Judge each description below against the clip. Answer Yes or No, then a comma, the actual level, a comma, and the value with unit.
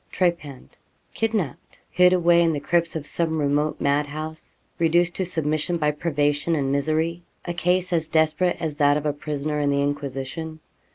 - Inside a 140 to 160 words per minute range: No, average, 170 wpm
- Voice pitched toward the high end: No, medium, 155 Hz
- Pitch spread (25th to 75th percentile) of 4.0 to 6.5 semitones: No, average, 2.8 semitones